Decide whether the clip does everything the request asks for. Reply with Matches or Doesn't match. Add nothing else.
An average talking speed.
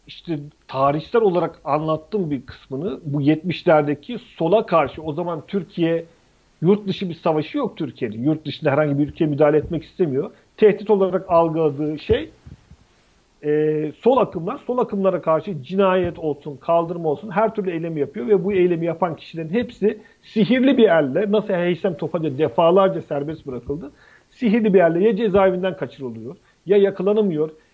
Doesn't match